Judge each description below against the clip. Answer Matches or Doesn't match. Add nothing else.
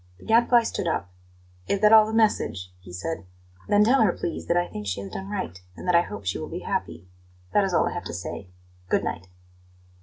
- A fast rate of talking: Matches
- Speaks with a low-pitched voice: Doesn't match